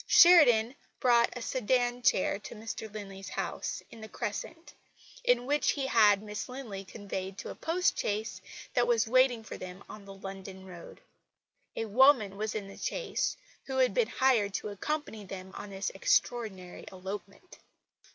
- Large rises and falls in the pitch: No, average, 4.3 semitones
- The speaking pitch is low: No, high, 220 Hz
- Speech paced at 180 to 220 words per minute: No, average, 160 wpm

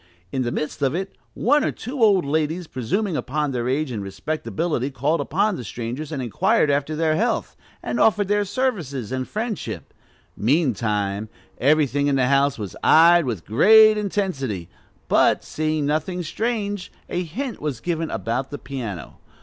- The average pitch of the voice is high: No, medium, 150 Hz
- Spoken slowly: No, average, 160 wpm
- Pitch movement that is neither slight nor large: No, wide, 6.3 semitones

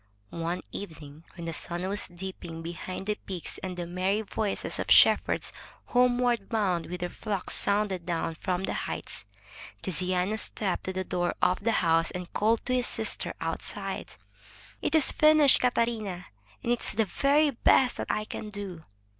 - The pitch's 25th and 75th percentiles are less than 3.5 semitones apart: No, average, 4.0 semitones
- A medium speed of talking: Yes, average, 165 wpm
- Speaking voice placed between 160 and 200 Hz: Yes, high, 190 Hz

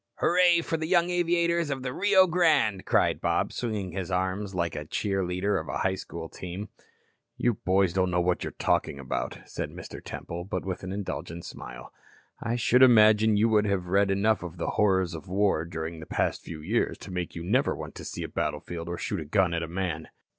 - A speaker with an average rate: No, fast, 210 wpm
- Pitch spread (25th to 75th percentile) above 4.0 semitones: Yes, average, 4.7 semitones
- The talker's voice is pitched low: Yes, very low, 95 Hz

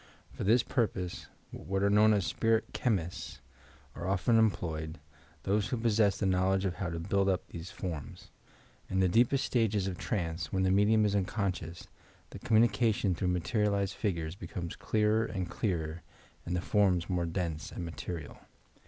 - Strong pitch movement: No, average, 3.5 semitones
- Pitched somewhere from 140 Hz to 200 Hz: No, very low, 95 Hz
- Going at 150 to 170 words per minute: Yes, average, 160 wpm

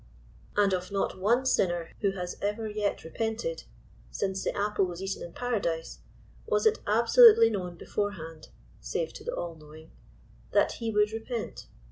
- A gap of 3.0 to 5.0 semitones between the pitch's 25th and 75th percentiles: Yes, average, 4.2 semitones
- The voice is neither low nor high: No, high, 205 Hz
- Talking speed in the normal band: Yes, average, 160 wpm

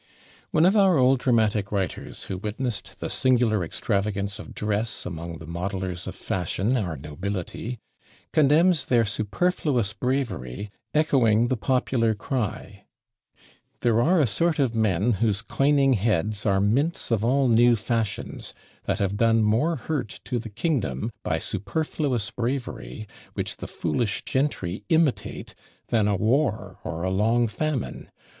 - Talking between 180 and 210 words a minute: No, average, 140 wpm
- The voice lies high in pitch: No, low, 115 Hz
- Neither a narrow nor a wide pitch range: Yes, average, 4.8 semitones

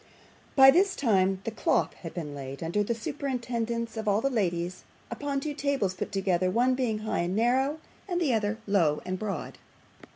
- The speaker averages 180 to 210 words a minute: Yes, average, 190 wpm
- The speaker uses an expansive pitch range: Yes, wide, 6.0 semitones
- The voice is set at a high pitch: Yes, high, 220 Hz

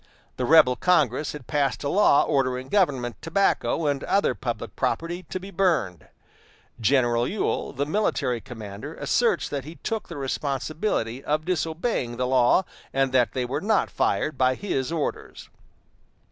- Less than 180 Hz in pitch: Yes, medium, 140 Hz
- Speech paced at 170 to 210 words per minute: No, average, 150 wpm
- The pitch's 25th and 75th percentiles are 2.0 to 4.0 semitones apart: No, average, 4.9 semitones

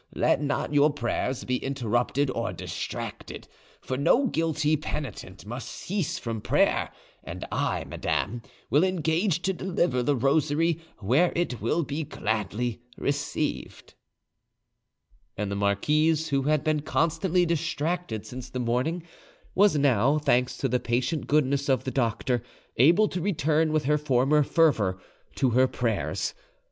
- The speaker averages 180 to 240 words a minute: No, average, 140 wpm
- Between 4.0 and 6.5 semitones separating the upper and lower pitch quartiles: Yes, average, 4.6 semitones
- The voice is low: No, medium, 145 Hz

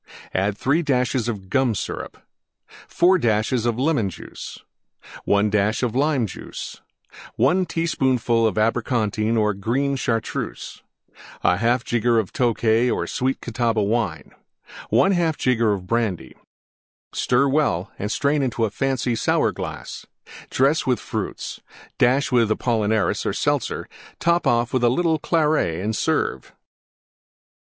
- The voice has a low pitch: Yes, low, 120 Hz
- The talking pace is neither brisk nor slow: No, slow, 115 wpm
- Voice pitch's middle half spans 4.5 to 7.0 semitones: No, average, 3.8 semitones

